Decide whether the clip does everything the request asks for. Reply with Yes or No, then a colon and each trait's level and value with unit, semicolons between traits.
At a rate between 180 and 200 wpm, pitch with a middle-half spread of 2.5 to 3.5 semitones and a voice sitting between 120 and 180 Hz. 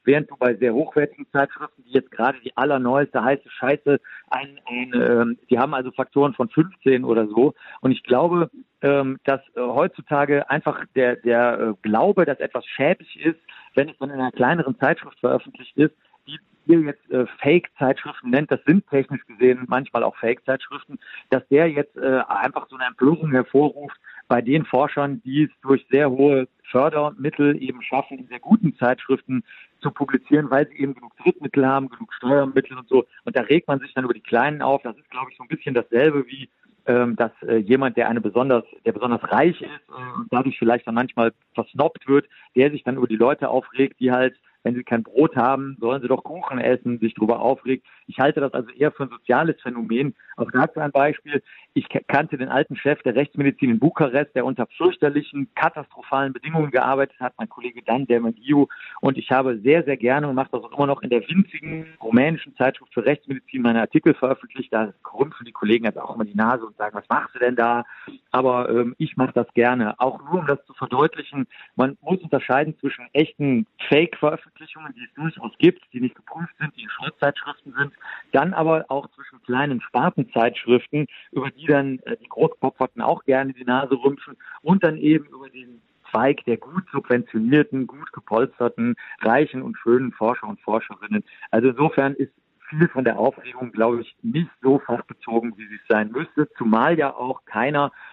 Yes: fast, 190 wpm; average, 3.0 semitones; low, 135 Hz